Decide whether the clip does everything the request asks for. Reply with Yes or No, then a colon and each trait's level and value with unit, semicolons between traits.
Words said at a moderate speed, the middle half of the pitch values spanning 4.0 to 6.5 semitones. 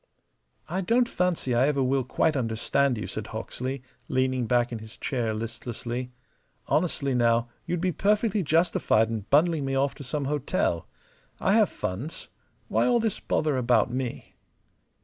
Yes: average, 155 wpm; average, 5.2 semitones